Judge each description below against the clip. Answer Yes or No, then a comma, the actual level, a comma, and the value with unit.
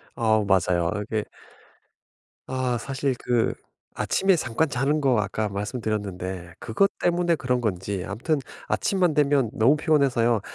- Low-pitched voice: Yes, low, 120 Hz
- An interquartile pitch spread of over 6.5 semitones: No, wide, 5.6 semitones